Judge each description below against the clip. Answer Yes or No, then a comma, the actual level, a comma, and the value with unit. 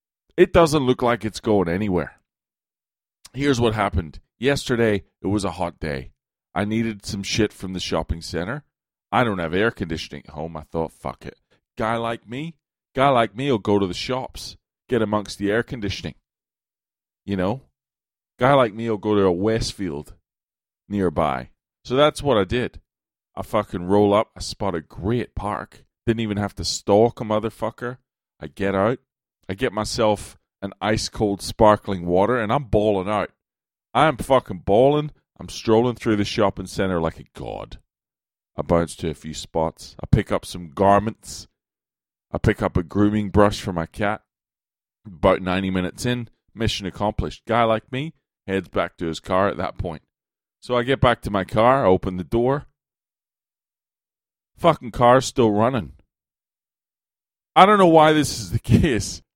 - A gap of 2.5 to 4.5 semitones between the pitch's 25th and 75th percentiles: Yes, average, 4.2 semitones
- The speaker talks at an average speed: Yes, average, 175 wpm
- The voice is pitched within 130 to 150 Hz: No, low, 105 Hz